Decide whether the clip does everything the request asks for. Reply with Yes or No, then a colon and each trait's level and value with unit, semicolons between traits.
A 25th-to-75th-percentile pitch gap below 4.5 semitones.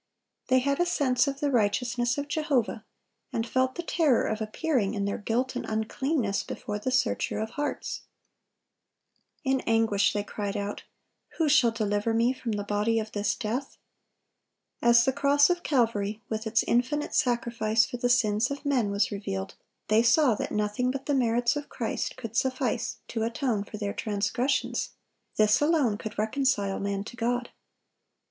Yes: average, 3.8 semitones